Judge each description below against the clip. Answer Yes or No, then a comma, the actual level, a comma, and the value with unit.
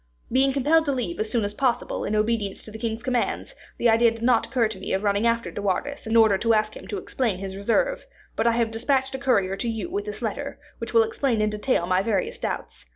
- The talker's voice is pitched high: Yes, high, 230 Hz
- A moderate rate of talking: No, fast, 250 wpm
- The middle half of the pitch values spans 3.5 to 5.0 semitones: Yes, average, 3.8 semitones